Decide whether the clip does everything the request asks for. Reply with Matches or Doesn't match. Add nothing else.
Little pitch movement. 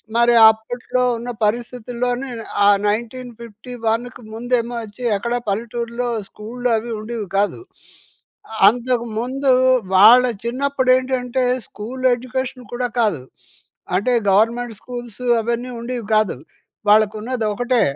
Matches